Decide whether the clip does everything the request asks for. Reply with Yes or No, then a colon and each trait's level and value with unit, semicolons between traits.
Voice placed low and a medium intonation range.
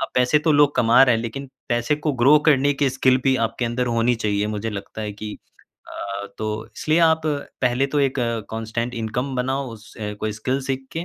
Yes: low, 125 Hz; average, 3.6 semitones